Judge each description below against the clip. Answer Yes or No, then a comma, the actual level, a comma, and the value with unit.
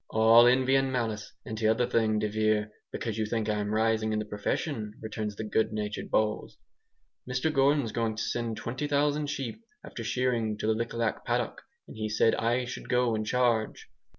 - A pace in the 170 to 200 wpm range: Yes, average, 185 wpm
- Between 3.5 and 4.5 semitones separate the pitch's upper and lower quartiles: No, narrow, 2.4 semitones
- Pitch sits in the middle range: No, low, 110 Hz